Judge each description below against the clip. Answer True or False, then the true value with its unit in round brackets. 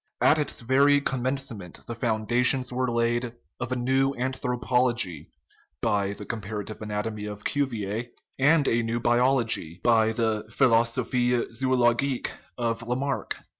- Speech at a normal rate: False (130 wpm)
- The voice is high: False (120 Hz)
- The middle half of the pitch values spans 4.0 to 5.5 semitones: False (2.6 semitones)